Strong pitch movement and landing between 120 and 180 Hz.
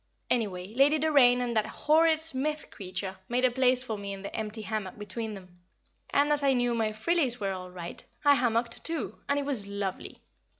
No: wide, 5.7 semitones; high, 235 Hz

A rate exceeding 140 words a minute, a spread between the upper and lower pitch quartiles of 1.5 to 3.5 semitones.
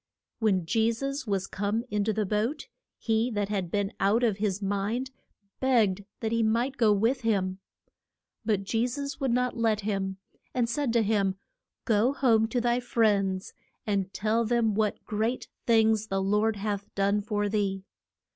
Yes: average, 170 wpm; narrow, 2.6 semitones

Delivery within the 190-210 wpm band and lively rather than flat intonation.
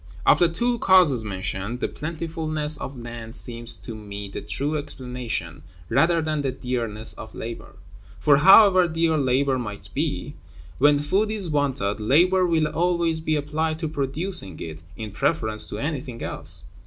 No: average, 155 wpm; wide, 6.1 semitones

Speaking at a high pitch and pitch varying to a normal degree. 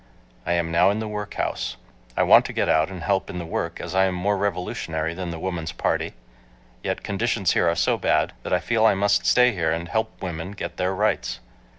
No: very low, 95 Hz; average, 3.4 semitones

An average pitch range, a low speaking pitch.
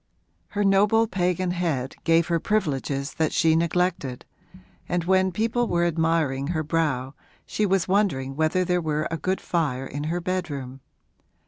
No: average, 3.8 semitones; medium, 170 Hz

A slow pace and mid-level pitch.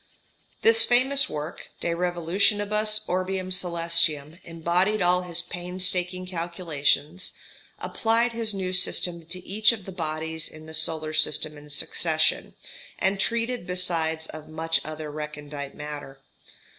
Yes: slow, 125 wpm; medium, 175 Hz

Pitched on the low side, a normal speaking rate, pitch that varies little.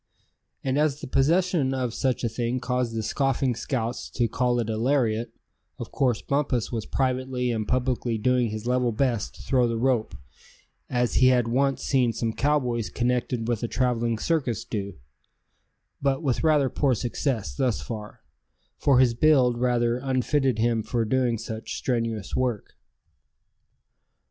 Yes: low, 125 Hz; average, 155 wpm; narrow, 2.3 semitones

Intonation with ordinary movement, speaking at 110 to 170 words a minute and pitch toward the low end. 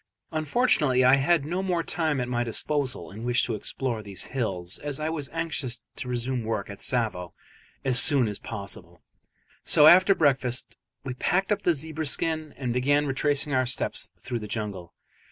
No: average, 4.7 semitones; average, 180 wpm; low, 130 Hz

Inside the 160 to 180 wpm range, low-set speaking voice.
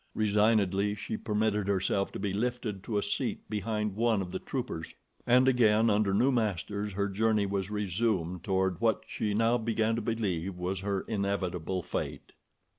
Yes: average, 165 wpm; low, 105 Hz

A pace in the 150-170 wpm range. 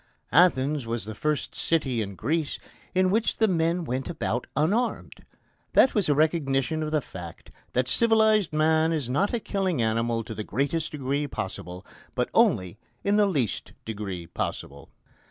Yes: average, 160 wpm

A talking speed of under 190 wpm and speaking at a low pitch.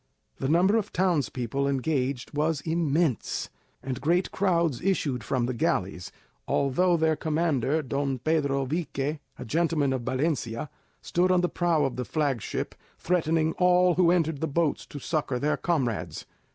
No: average, 150 wpm; medium, 150 Hz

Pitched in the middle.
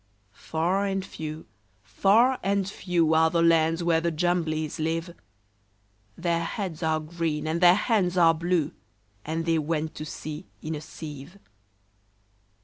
Yes: medium, 165 Hz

